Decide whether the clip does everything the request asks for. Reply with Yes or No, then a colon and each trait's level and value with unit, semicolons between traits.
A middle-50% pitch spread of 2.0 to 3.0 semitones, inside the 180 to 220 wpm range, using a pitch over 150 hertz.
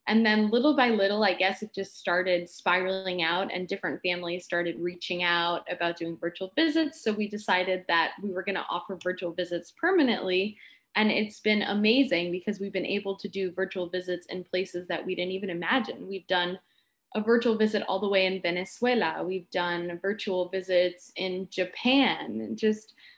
Yes: average, 2.7 semitones; average, 185 wpm; medium, 185 Hz